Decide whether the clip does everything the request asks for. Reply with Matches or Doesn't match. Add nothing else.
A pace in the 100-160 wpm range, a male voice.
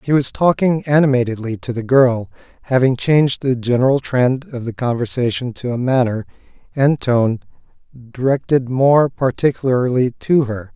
Matches